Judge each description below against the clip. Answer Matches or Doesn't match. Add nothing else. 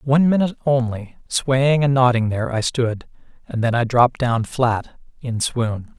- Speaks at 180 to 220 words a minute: Doesn't match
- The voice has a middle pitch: Doesn't match